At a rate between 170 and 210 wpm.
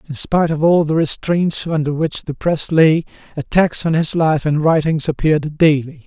Yes: average, 190 wpm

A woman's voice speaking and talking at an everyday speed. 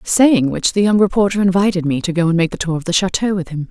No: female; fast, 290 wpm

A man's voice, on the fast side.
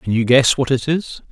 Yes: male; fast, 275 wpm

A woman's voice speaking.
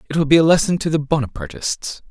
No: male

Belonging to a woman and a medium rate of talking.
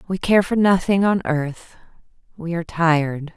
Yes: female; average, 160 wpm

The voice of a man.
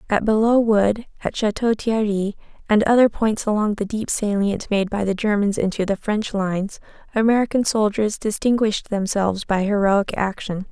No: female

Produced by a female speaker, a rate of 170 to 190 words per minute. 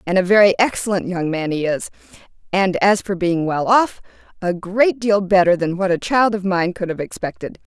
No: female; average, 200 wpm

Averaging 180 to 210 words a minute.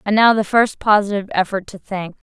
Yes: fast, 205 wpm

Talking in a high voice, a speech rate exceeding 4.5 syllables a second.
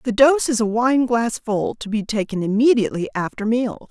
Yes: high, 230 Hz; 5.1 syllables/s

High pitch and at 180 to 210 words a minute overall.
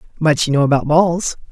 No: medium, 155 Hz; average, 200 wpm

